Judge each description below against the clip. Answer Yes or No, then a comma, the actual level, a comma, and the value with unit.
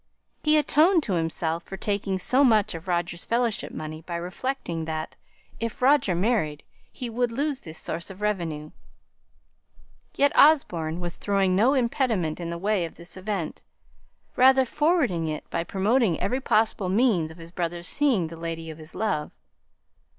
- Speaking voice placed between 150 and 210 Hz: Yes, high, 190 Hz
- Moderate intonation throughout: No, wide, 6.6 semitones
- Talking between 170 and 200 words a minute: No, average, 160 wpm